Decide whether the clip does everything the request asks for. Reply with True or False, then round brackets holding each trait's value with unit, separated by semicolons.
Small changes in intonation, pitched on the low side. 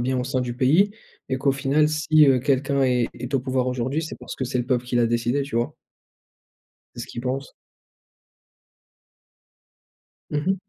True (2.2 semitones; 130 Hz)